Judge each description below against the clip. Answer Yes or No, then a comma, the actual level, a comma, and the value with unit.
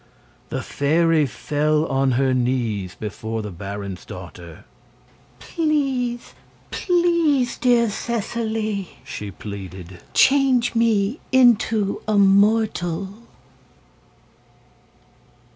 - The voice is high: Yes, high, 195 Hz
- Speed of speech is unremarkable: No, slow, 80 wpm